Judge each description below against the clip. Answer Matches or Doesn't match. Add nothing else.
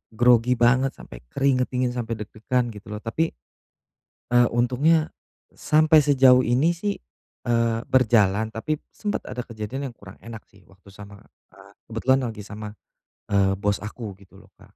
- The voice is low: Matches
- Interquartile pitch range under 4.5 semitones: Matches